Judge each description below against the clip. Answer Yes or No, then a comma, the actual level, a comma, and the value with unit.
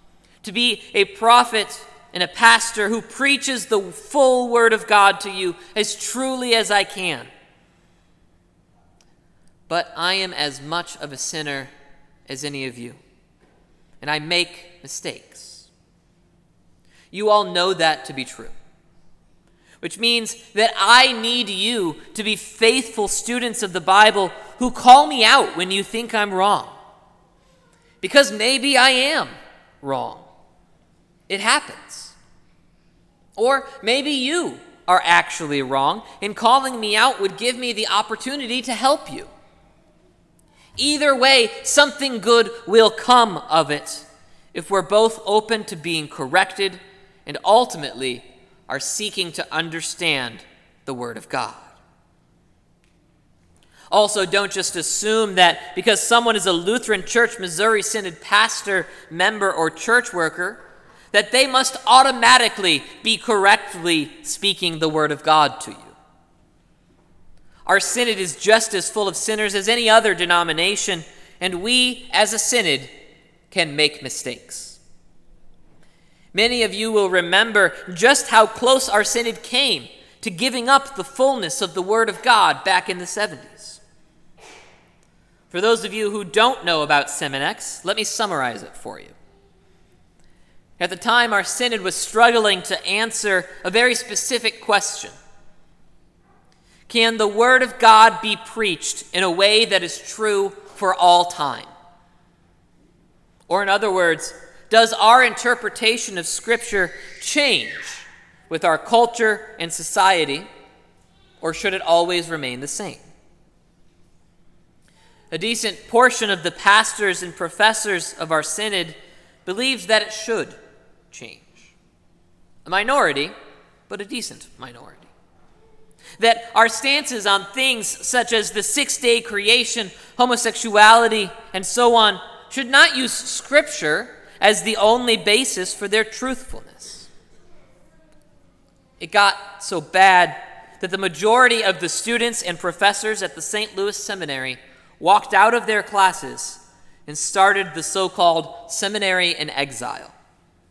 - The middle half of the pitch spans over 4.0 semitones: Yes, average, 5.0 semitones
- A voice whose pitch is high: Yes, high, 205 Hz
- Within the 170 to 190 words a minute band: No, slow, 135 wpm